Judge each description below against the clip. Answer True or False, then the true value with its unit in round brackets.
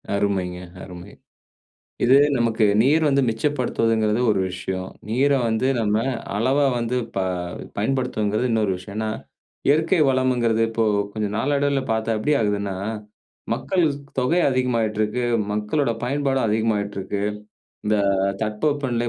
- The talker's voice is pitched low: True (115 Hz)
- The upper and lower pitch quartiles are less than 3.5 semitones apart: False (4.0 semitones)